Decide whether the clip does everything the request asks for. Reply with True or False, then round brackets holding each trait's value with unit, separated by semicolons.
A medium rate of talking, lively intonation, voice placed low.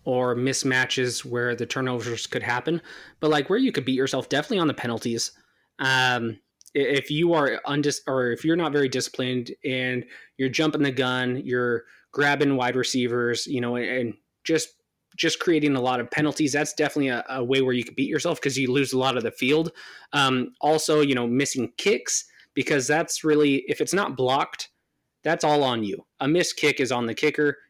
False (195 wpm; 3.1 semitones; 130 Hz)